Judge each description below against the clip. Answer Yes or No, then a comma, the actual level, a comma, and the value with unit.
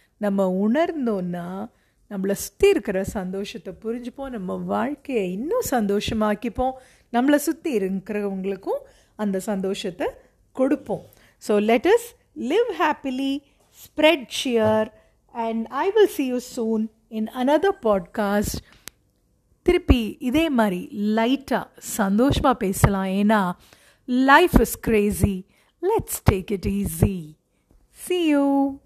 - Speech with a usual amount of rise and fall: No, wide, 5.7 semitones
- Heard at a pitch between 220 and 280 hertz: Yes, high, 225 Hz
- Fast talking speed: No, average, 100 wpm